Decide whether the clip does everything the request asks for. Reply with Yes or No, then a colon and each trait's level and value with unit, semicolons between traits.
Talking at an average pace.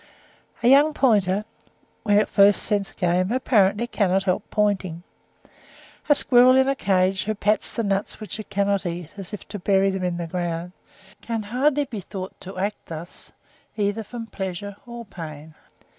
Yes: average, 170 wpm